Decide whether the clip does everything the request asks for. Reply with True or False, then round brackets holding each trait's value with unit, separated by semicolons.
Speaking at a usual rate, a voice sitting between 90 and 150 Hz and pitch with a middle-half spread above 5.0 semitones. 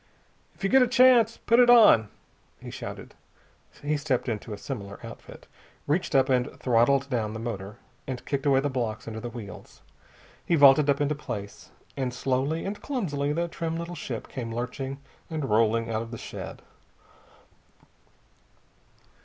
True (160 wpm; 135 Hz; 5.4 semitones)